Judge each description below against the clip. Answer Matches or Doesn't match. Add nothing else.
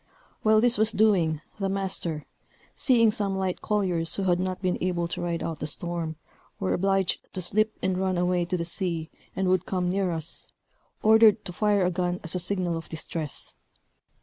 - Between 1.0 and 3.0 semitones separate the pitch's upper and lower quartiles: Matches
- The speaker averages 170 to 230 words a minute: Matches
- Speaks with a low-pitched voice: Doesn't match